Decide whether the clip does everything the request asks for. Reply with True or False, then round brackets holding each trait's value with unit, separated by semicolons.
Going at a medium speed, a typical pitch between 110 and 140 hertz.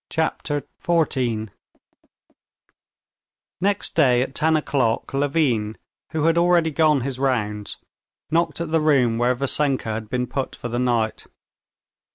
False (130 wpm; 135 Hz)